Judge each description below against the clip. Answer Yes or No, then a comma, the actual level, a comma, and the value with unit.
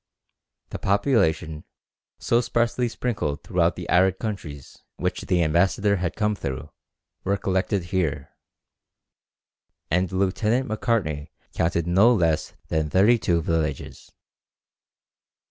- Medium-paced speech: No, slow, 110 wpm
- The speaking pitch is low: Yes, very low, 95 Hz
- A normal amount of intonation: Yes, average, 4.9 semitones